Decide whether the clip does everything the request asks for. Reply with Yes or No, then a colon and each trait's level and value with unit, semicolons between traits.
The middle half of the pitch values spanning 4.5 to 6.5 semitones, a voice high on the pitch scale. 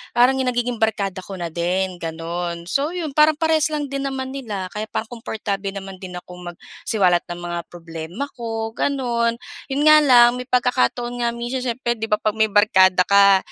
Yes: average, 5.2 semitones; high, 220 Hz